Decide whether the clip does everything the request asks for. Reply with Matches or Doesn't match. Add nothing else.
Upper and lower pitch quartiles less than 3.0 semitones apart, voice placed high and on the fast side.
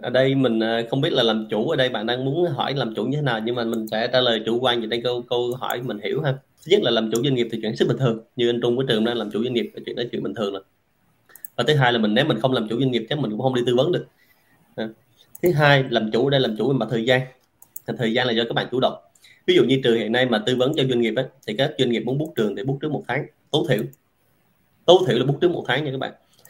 Doesn't match